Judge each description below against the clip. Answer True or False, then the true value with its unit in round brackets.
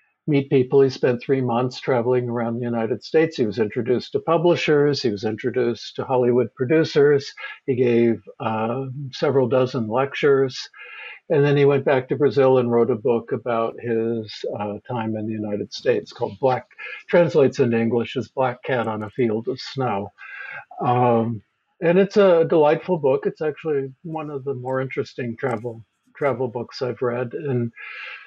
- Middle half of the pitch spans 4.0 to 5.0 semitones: False (3.1 semitones)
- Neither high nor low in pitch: False (125 Hz)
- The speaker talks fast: False (170 wpm)